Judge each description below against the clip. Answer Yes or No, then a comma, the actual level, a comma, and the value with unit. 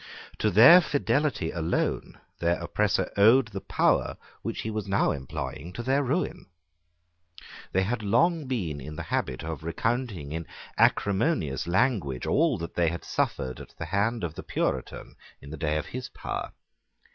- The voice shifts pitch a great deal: Yes, wide, 7.1 semitones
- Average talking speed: Yes, average, 160 wpm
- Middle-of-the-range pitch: No, low, 100 Hz